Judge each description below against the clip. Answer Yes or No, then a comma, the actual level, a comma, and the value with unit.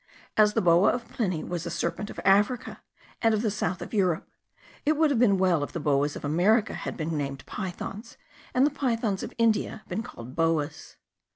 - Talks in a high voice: Yes, high, 195 Hz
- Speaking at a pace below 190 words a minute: No, average, 200 wpm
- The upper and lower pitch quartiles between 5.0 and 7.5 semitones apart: Yes, wide, 5.4 semitones